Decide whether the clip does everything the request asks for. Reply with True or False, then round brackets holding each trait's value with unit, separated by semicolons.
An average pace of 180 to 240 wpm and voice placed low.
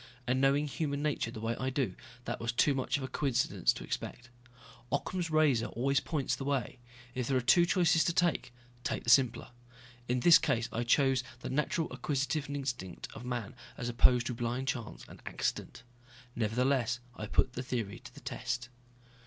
True (185 wpm; 130 Hz)